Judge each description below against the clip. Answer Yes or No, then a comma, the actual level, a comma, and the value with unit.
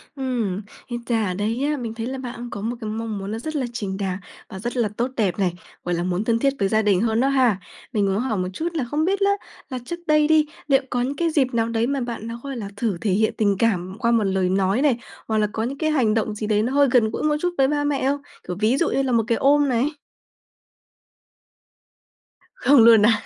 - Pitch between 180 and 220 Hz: No, high, 230 Hz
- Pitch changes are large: No, average, 4.5 semitones